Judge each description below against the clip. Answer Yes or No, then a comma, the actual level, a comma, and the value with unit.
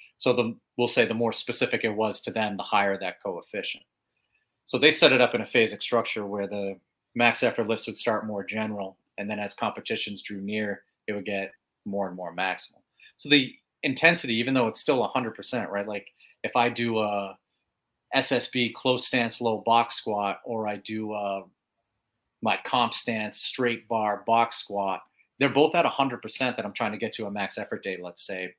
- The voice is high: No, low, 110 Hz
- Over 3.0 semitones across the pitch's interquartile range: No, average, 2.7 semitones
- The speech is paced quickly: No, average, 195 wpm